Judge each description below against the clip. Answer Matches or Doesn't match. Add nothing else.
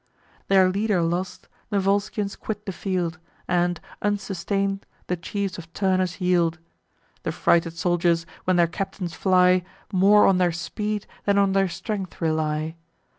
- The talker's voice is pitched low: Doesn't match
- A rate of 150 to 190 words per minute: Doesn't match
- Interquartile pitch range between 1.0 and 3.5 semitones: Matches